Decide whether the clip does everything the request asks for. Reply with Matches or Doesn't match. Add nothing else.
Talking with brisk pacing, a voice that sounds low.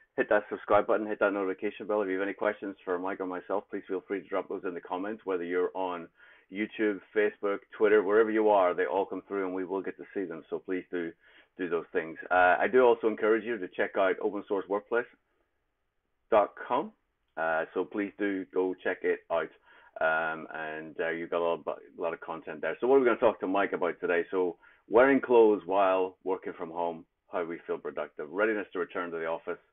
Matches